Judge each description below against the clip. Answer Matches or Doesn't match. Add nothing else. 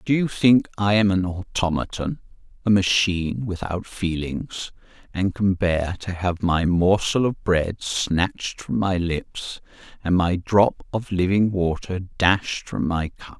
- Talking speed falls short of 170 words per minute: Matches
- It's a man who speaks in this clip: Matches